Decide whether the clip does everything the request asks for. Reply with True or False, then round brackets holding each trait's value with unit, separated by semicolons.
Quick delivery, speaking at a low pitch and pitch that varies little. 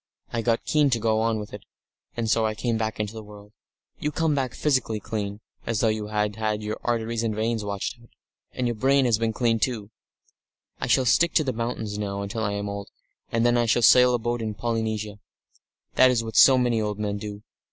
True (225 wpm; 110 Hz; 2.2 semitones)